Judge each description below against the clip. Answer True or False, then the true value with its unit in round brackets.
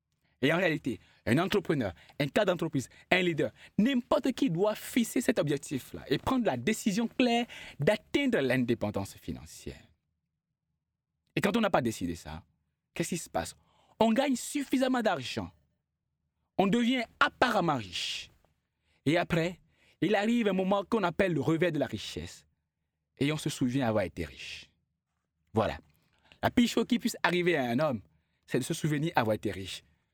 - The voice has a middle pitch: True (150 Hz)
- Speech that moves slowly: False (160 wpm)